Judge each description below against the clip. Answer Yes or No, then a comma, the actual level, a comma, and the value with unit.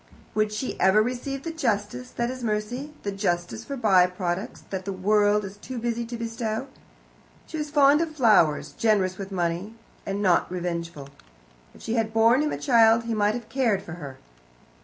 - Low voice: No, high, 215 Hz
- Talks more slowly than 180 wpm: No, average, 185 wpm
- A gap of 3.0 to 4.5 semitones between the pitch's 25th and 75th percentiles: Yes, average, 4.2 semitones